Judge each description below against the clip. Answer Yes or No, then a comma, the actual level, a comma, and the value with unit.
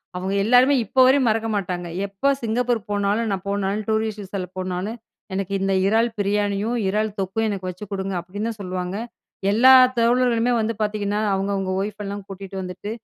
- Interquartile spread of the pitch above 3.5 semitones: No, narrow, 2.6 semitones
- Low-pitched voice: No, high, 205 Hz